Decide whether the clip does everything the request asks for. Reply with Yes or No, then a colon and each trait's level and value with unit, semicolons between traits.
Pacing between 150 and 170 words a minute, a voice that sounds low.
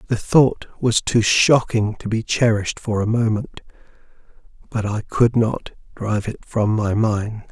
Yes: average, 160 wpm; low, 110 Hz